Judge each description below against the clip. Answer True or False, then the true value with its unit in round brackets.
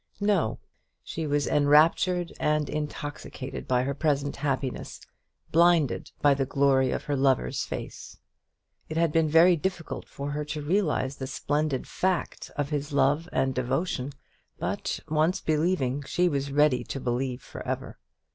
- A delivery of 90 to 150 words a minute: True (145 wpm)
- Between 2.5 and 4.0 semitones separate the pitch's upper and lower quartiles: True (3.0 semitones)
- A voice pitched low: False (145 Hz)